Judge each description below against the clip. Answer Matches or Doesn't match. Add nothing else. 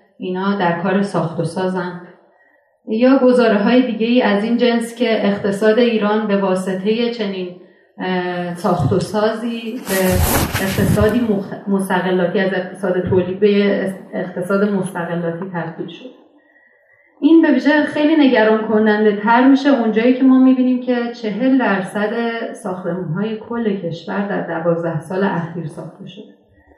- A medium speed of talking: Matches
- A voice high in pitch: Matches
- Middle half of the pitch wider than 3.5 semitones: Matches